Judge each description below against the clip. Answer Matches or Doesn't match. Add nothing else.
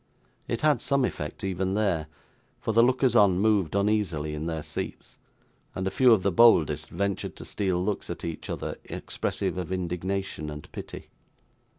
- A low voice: Matches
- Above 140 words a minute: Matches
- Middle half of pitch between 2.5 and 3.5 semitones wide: Doesn't match